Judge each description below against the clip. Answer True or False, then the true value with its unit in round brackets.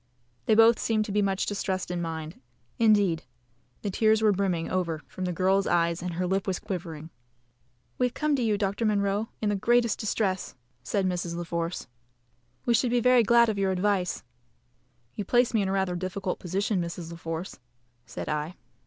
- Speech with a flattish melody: False (3.5 semitones)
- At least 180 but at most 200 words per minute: True (190 wpm)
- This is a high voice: True (195 Hz)